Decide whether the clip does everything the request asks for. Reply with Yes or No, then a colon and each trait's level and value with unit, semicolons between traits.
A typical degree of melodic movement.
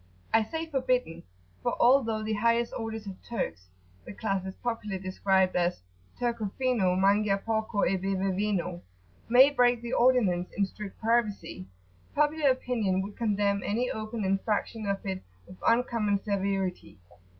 Yes: average, 3.5 semitones